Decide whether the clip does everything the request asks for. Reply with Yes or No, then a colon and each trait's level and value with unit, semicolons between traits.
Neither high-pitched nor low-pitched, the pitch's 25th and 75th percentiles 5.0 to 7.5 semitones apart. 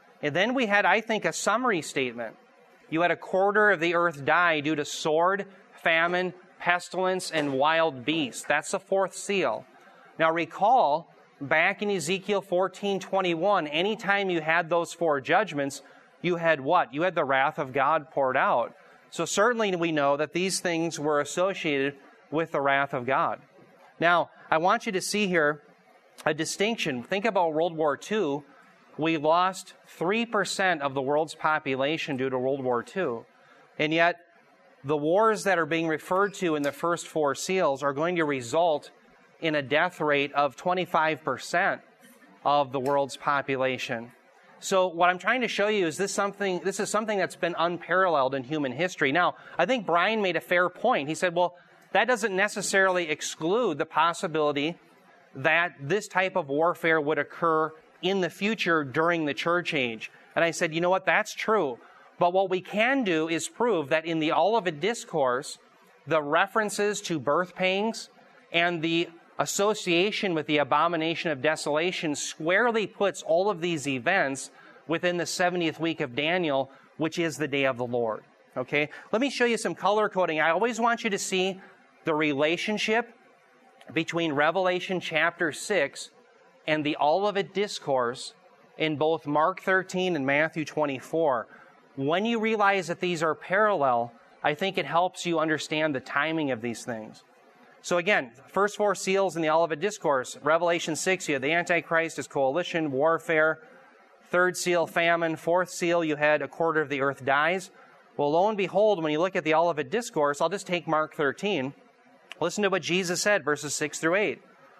No: medium, 170 Hz; average, 4.0 semitones